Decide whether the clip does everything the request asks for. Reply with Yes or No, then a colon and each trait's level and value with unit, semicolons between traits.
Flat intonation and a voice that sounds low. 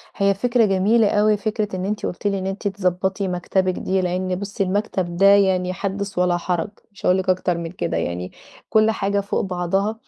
No: narrow, 1.9 semitones; high, 190 Hz